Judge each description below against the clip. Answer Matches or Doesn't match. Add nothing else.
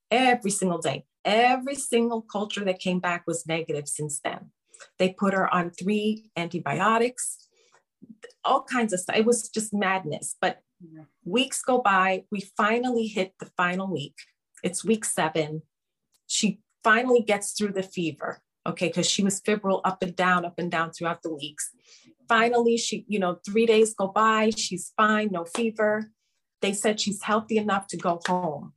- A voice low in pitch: Doesn't match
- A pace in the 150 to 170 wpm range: Matches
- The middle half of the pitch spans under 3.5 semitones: Doesn't match